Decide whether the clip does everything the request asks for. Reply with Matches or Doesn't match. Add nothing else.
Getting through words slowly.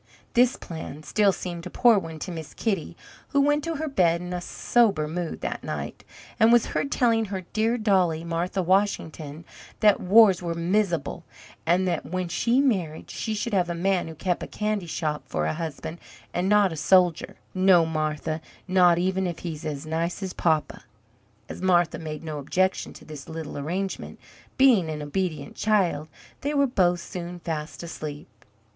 Doesn't match